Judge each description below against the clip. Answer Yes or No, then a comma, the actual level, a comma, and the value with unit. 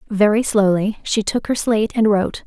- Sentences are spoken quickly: No, average, 195 wpm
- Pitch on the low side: No, high, 210 Hz